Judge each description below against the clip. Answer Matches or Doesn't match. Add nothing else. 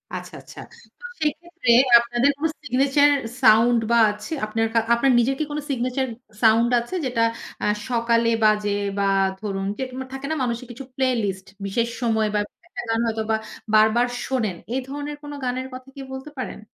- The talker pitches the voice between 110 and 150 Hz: Doesn't match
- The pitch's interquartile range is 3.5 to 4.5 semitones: Doesn't match